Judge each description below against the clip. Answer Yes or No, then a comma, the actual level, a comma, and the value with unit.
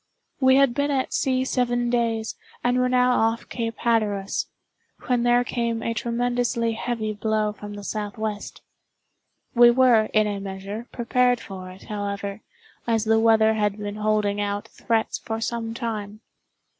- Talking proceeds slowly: No, average, 155 wpm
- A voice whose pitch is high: Yes, high, 225 Hz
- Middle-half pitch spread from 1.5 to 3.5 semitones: Yes, narrow, 2.5 semitones